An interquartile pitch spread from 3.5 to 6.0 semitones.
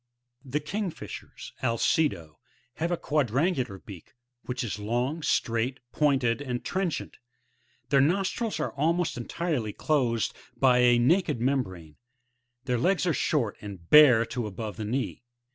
Yes: average, 5.1 semitones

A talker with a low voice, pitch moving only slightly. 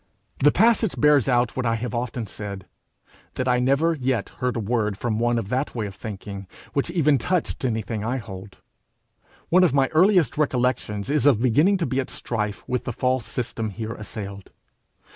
No: low, 125 Hz; average, 4.4 semitones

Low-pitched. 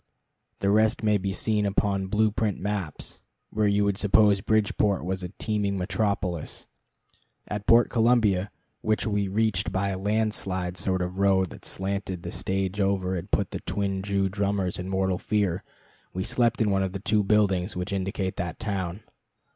Yes: low, 100 Hz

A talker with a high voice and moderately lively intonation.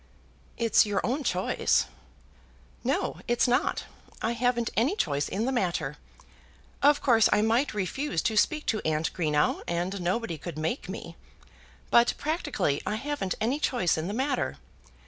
No: high, 225 Hz; wide, 6.5 semitones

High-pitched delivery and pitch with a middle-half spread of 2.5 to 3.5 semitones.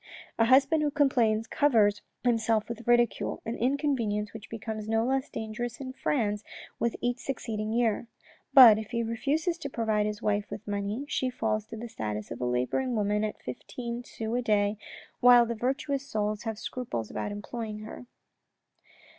Yes: high, 225 Hz; average, 2.8 semitones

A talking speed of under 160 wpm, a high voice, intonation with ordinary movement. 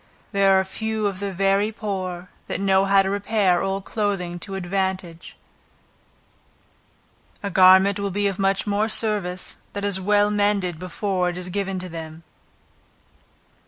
No: average, 150 wpm; high, 195 Hz; narrow, 1.8 semitones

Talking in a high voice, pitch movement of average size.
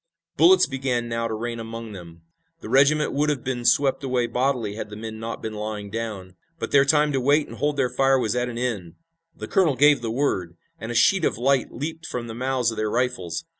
No: low, 120 Hz; average, 3.6 semitones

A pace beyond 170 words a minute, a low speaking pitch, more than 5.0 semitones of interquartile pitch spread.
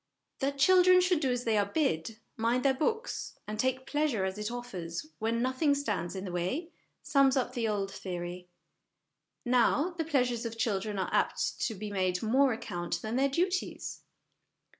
No: average, 180 wpm; high, 240 Hz; wide, 5.6 semitones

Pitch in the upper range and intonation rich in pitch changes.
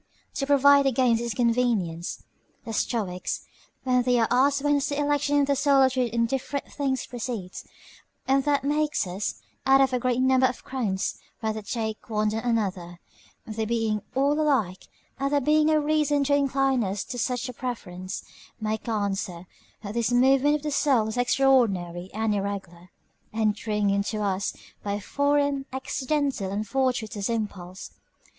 No: high, 245 Hz; average, 4.6 semitones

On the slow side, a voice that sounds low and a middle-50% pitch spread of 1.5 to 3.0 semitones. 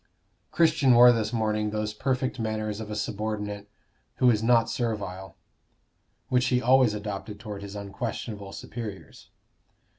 Yes: slow, 130 wpm; low, 110 Hz; narrow, 2.6 semitones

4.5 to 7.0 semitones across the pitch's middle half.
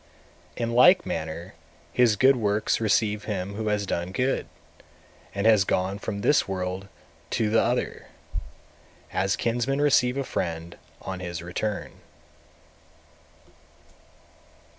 No: average, 4.1 semitones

